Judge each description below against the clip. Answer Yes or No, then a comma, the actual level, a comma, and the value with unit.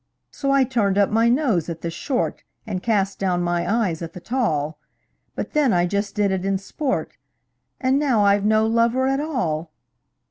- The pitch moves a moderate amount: No, wide, 6.0 semitones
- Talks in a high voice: Yes, high, 205 Hz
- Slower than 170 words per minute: No, average, 185 wpm